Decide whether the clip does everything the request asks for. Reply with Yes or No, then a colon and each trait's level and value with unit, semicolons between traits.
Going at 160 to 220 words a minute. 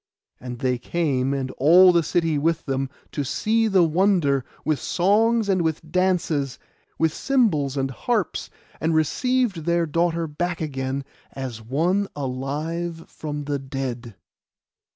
No: slow, 135 wpm